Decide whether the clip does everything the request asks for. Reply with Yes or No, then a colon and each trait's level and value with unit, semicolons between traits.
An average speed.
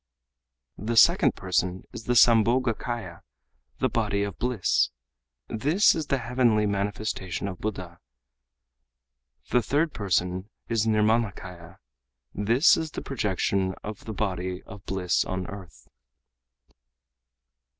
No: slow, 115 wpm